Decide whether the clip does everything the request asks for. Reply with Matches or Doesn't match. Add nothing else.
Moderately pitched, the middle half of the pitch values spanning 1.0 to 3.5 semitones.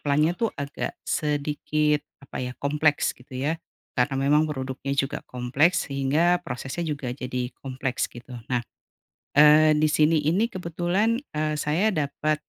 Matches